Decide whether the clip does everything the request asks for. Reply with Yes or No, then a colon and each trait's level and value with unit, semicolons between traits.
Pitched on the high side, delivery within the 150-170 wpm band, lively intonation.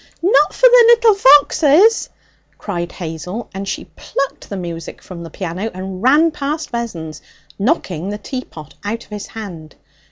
Yes: high, 210 Hz; average, 155 wpm; wide, 8.7 semitones